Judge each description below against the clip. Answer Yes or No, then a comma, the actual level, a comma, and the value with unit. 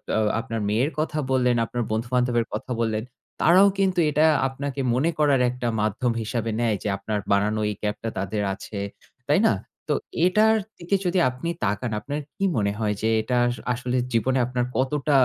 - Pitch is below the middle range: Yes, low, 125 Hz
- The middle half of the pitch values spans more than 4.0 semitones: Yes, average, 4.5 semitones